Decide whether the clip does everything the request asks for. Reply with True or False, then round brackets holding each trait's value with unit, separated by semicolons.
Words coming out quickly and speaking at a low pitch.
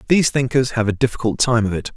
True (245 wpm; 120 Hz)